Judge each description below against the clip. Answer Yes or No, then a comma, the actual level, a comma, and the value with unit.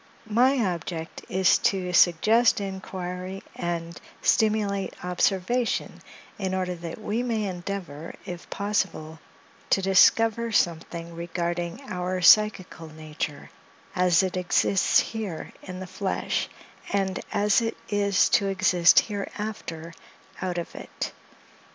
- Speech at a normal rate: No, slow, 115 wpm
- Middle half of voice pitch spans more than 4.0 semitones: No, average, 3.0 semitones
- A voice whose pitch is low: No, medium, 185 Hz